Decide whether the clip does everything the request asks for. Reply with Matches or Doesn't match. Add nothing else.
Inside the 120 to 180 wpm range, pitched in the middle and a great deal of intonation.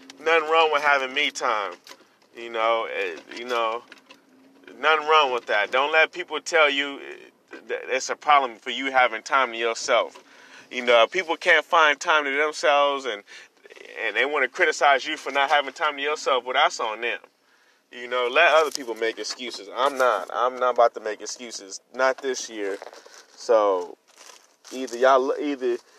Matches